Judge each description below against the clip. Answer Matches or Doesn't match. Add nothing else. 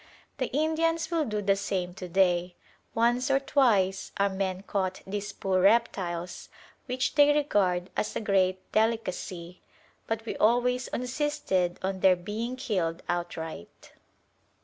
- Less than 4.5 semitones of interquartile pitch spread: Doesn't match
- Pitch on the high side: Matches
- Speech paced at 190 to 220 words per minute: Doesn't match